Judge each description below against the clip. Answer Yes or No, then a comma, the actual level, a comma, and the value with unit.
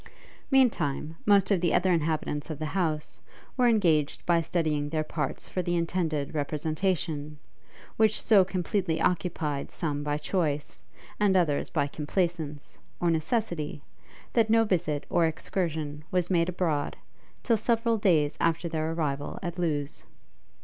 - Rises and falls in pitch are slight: No, average, 3.6 semitones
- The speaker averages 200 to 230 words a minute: No, average, 140 wpm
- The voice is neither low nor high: Yes, medium, 165 Hz